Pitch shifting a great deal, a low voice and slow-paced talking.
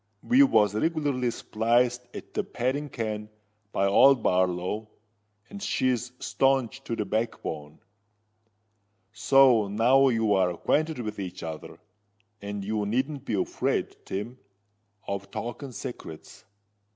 No: average, 4.5 semitones; low, 115 Hz; slow, 115 wpm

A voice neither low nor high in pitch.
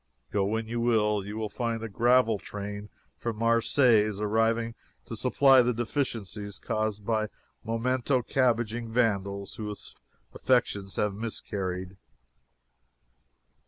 No: low, 110 Hz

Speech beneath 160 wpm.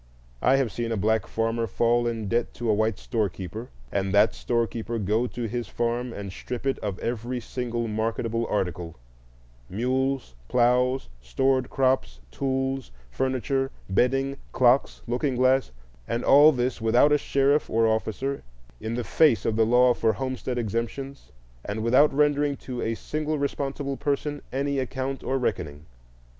Yes: average, 150 wpm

